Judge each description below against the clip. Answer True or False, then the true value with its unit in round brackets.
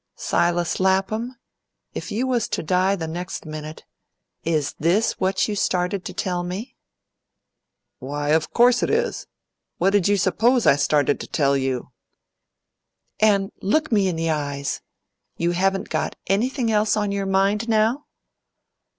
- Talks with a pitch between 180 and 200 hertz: True (190 Hz)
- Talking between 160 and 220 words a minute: False (150 wpm)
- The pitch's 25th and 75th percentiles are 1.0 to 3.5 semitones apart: False (4.8 semitones)